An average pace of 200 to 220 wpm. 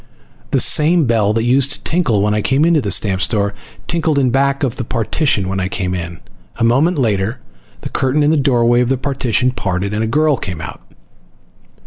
Yes: fast, 205 wpm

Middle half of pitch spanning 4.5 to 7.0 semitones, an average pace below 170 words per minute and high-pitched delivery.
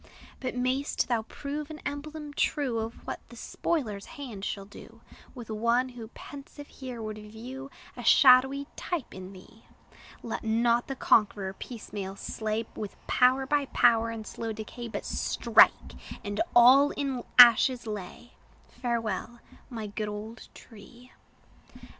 No: average, 3.4 semitones; average, 140 wpm; high, 235 Hz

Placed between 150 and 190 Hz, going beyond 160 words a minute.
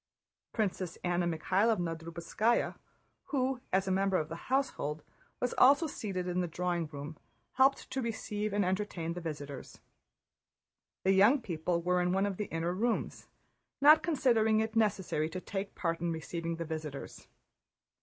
No: medium, 185 Hz; average, 155 wpm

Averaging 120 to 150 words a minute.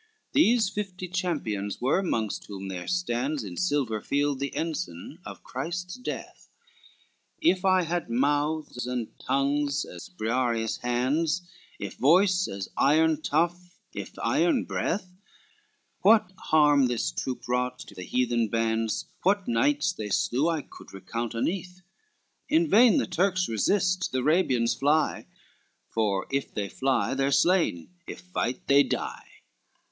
Yes: average, 140 wpm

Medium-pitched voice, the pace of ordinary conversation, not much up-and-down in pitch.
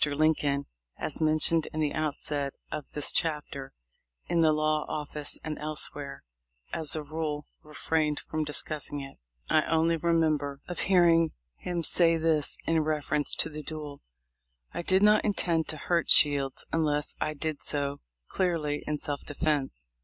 Yes: medium, 155 Hz; average, 150 wpm; narrow, 1.9 semitones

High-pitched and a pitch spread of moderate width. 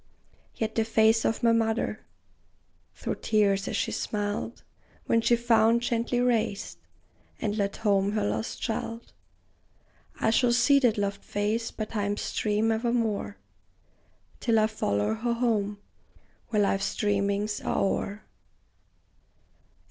No: high, 220 Hz; narrow, 2.0 semitones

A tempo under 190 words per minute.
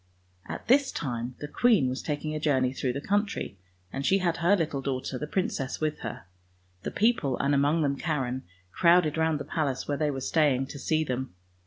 No: average, 200 wpm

